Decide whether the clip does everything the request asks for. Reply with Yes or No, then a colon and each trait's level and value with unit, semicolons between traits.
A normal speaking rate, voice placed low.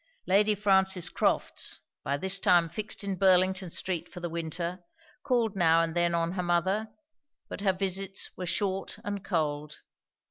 No: average, 155 wpm; medium, 185 Hz